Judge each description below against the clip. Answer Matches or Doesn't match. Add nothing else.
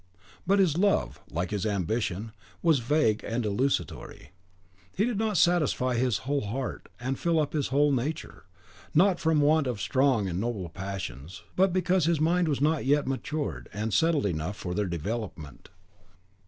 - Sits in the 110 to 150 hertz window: Matches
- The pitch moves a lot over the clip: Matches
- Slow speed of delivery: Doesn't match